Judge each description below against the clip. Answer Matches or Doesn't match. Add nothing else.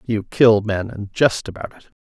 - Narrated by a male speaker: Matches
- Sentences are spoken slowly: Doesn't match